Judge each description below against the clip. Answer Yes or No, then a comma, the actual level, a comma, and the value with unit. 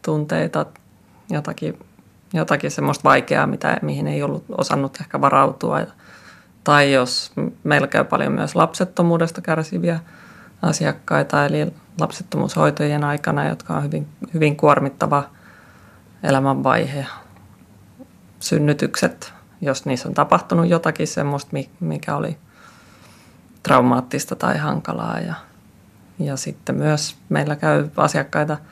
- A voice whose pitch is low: No, medium, 150 Hz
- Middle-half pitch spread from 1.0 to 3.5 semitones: No, average, 3.9 semitones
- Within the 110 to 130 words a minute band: No, average, 100 wpm